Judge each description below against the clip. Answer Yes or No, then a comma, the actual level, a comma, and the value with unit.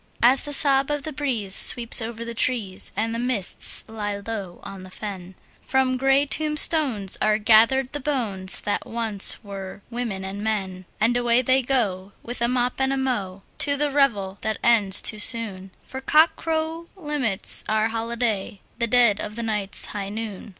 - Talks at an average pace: Yes, average, 170 wpm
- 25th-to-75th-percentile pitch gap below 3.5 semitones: No, average, 4.6 semitones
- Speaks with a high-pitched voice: Yes, high, 230 Hz